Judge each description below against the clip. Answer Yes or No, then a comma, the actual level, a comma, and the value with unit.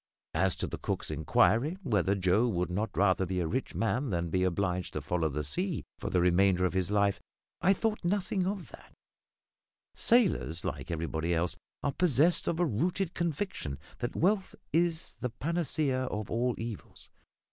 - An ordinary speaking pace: Yes, average, 170 wpm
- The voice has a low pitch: Yes, low, 110 Hz